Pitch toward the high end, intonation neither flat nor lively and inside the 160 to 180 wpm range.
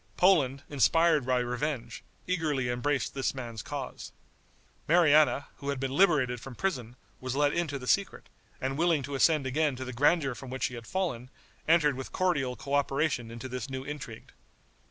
No: low, 135 Hz; average, 3.3 semitones; average, 170 wpm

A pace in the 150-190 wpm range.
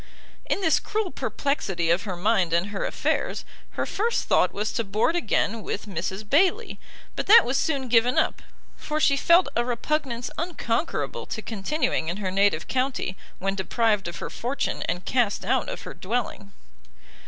Yes: average, 170 wpm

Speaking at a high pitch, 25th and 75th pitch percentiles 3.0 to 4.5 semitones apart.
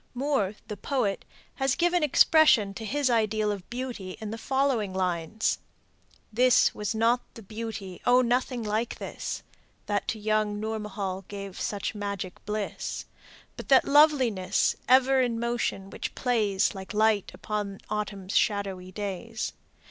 Yes: high, 215 Hz; average, 3.6 semitones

